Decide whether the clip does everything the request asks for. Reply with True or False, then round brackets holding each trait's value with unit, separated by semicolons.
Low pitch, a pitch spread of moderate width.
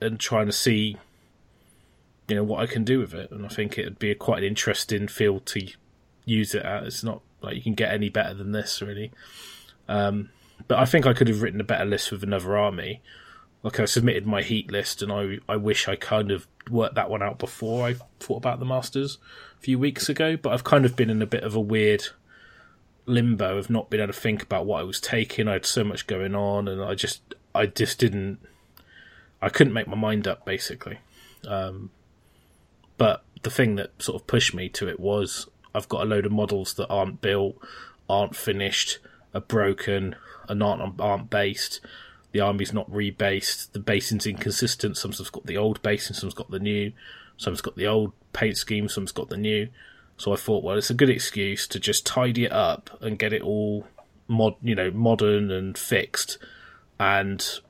False (105 Hz; 2.0 semitones)